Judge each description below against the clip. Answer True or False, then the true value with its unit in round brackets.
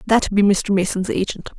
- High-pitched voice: True (200 Hz)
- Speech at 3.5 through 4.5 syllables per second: False (5.0 syllables/s)